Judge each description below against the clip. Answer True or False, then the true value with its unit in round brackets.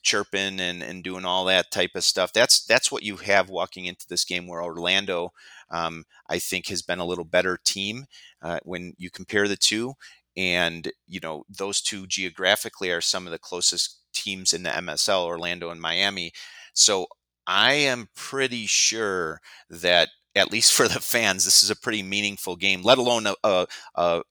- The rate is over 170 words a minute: True (185 wpm)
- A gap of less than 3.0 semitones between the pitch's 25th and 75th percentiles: True (2.4 semitones)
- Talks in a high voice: False (95 Hz)